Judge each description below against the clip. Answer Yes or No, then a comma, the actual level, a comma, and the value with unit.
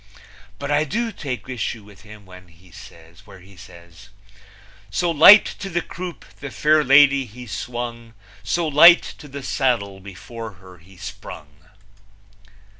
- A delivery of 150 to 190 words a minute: No, slow, 135 wpm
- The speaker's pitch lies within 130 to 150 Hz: No, low, 115 Hz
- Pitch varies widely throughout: Yes, wide, 7.5 semitones